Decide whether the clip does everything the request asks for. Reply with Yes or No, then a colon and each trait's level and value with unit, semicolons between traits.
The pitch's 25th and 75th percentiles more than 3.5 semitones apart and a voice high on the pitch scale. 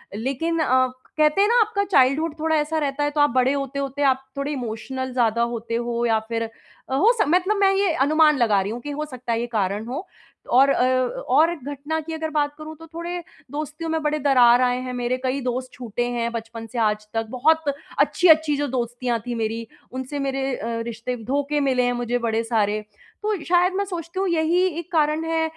Yes: average, 4.7 semitones; very high, 270 Hz